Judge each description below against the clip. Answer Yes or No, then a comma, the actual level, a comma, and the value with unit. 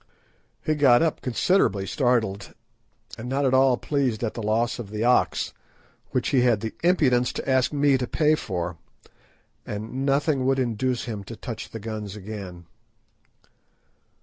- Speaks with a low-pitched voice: Yes, low, 120 Hz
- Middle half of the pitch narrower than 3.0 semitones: No, average, 3.9 semitones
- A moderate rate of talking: Yes, average, 155 wpm